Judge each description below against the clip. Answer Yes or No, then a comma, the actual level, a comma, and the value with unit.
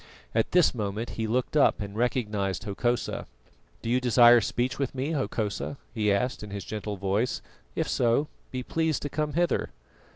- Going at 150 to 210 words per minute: Yes, average, 170 wpm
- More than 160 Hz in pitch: No, low, 120 Hz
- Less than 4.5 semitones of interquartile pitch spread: Yes, average, 3.8 semitones